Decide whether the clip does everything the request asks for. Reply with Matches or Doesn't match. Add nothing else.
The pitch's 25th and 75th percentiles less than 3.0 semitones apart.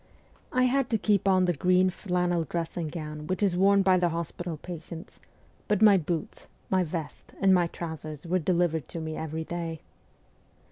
Matches